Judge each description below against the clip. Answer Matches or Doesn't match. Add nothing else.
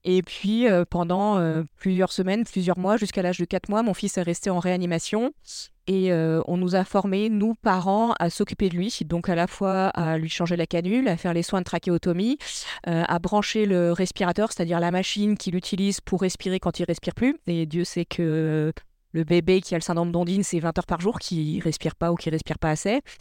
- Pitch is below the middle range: Doesn't match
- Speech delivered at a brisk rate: Matches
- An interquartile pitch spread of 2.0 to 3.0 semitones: Matches